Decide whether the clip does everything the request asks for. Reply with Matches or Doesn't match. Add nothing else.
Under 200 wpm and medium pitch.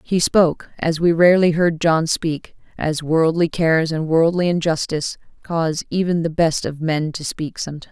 Matches